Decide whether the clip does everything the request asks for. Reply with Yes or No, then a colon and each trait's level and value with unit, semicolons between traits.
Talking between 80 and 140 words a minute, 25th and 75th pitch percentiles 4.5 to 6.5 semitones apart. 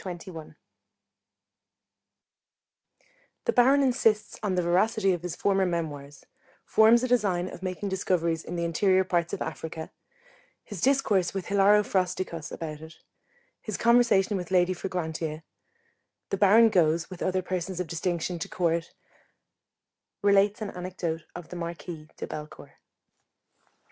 No: slow, 135 wpm; average, 3.0 semitones